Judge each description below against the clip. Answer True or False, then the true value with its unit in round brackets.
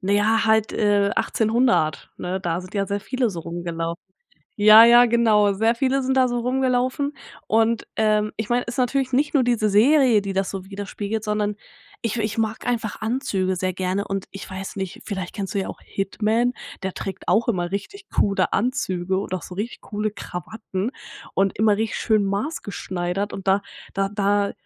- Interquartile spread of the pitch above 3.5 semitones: False (3.2 semitones)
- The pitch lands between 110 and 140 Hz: False (210 Hz)